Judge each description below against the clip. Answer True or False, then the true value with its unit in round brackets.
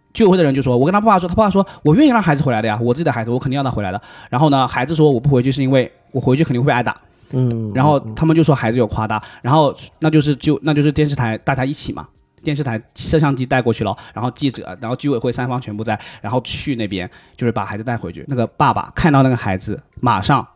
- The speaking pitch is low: True (130 Hz)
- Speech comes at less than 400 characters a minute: False (410 characters per minute)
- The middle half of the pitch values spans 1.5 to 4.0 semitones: False (4.9 semitones)